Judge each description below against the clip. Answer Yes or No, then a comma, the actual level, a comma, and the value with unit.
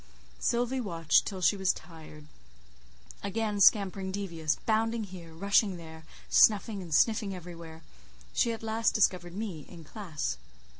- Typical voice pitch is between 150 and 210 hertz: Yes, high, 190 Hz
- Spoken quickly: No, slow, 135 wpm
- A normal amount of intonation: Yes, average, 4.6 semitones